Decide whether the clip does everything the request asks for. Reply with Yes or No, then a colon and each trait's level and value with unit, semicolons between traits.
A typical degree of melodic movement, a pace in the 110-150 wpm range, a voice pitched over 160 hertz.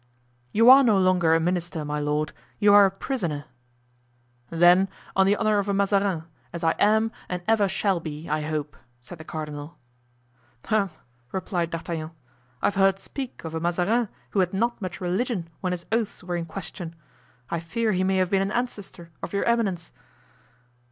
No: average, 3.6 semitones; average, 180 wpm; medium, 185 Hz